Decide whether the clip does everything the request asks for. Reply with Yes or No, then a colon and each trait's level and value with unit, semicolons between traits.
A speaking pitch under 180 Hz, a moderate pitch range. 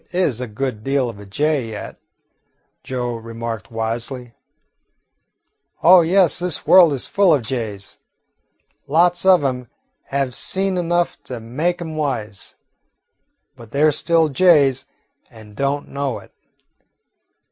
No: low, 135 Hz; wide, 6.2 semitones